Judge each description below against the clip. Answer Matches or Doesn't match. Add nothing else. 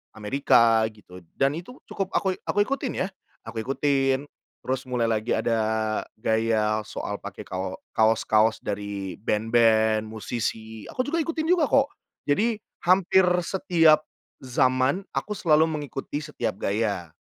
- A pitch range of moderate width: Doesn't match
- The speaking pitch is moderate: Doesn't match